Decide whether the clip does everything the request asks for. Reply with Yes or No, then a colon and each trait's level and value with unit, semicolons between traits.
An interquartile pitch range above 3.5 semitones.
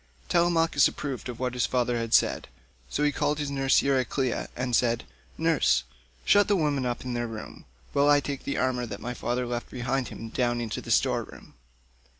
No: average, 3.0 semitones